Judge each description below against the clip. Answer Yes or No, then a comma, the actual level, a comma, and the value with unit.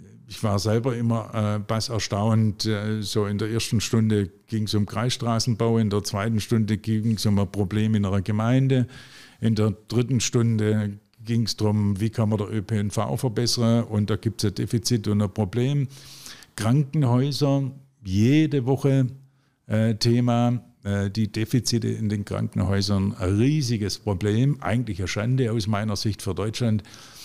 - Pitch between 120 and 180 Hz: No, low, 110 Hz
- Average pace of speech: Yes, average, 160 wpm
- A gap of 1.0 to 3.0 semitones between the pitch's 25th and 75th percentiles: Yes, narrow, 2.6 semitones